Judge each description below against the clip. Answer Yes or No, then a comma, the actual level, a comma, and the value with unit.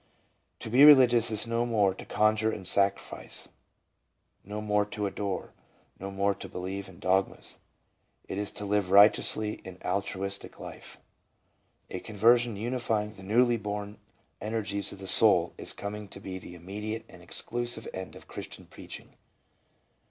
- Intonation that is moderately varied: No, narrow, 2.2 semitones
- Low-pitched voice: Yes, low, 105 Hz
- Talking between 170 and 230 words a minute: No, average, 150 wpm